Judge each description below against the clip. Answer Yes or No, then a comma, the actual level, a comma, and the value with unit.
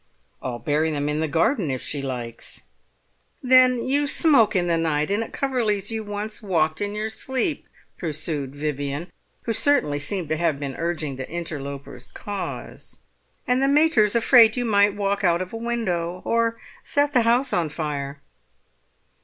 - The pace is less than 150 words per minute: No, average, 165 wpm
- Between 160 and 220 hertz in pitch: Yes, medium, 185 Hz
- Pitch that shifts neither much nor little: No, wide, 7.3 semitones